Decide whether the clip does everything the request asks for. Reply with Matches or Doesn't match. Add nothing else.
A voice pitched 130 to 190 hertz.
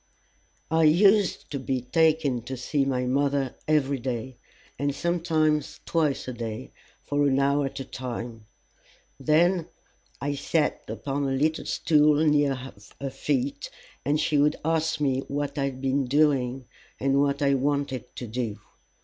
Matches